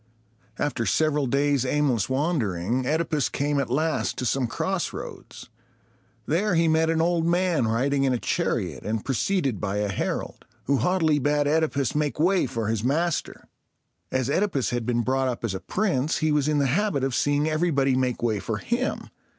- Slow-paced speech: No, average, 175 wpm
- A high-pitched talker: No, medium, 140 Hz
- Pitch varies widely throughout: No, average, 4.3 semitones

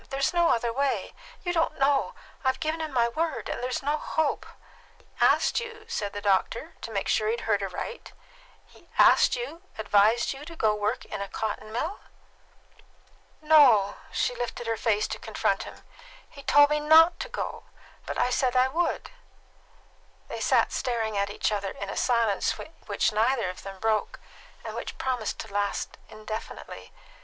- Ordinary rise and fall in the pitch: No, wide, 5.9 semitones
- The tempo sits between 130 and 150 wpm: No, average, 180 wpm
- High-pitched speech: Yes, high, 240 Hz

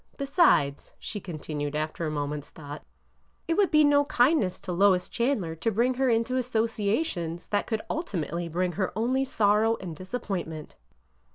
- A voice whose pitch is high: Yes, high, 200 Hz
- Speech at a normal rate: Yes, average, 160 wpm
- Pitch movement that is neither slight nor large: No, wide, 7.2 semitones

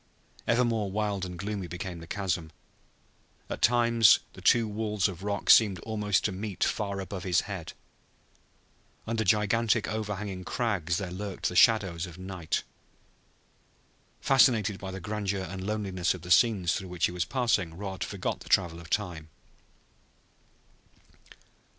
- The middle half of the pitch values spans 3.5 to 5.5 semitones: No, average, 3.0 semitones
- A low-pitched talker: Yes, low, 100 Hz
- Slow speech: No, average, 145 wpm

